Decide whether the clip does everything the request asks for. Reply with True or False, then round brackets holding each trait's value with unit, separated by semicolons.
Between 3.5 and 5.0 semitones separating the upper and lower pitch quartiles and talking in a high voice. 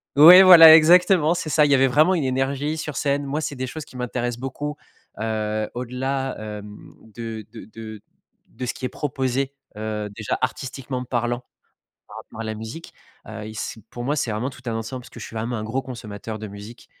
False (4.2 semitones; 125 Hz)